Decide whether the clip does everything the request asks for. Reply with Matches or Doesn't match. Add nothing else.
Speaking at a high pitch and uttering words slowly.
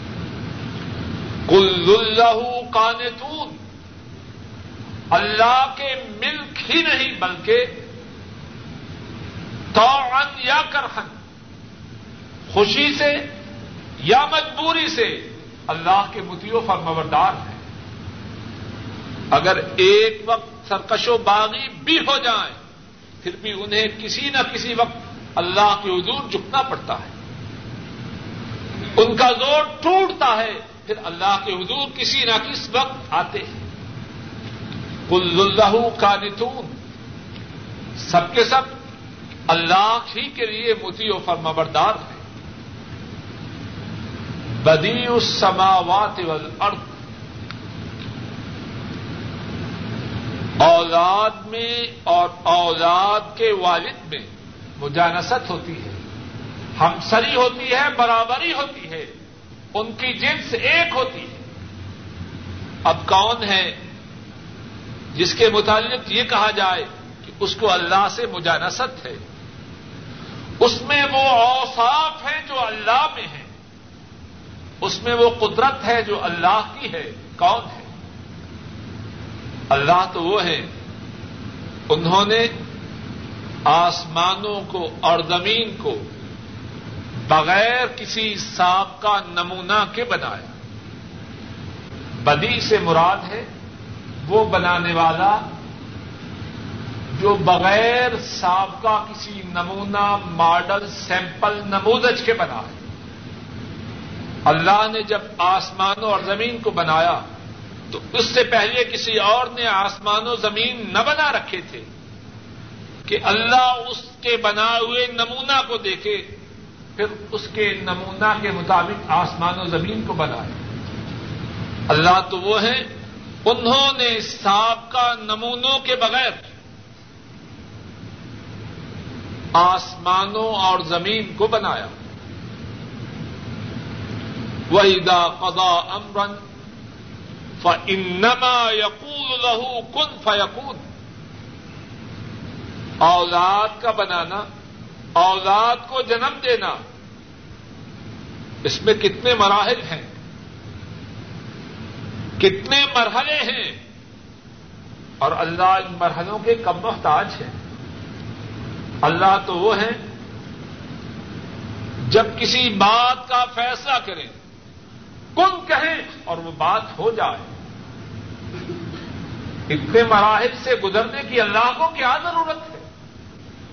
Matches